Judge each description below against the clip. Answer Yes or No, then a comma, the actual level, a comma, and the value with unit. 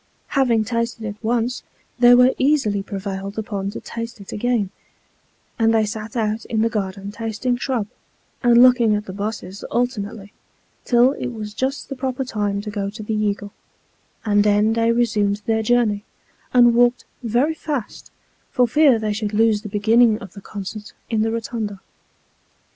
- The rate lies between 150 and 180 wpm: Yes, average, 165 wpm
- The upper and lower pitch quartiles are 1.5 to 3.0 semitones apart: Yes, average, 2.7 semitones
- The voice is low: No, high, 220 Hz